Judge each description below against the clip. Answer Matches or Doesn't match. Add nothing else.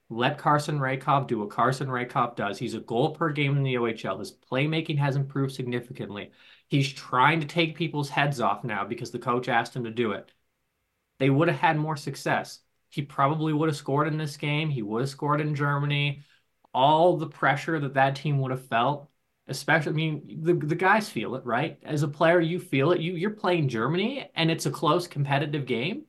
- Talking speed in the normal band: Doesn't match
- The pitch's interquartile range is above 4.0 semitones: Doesn't match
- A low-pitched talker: Doesn't match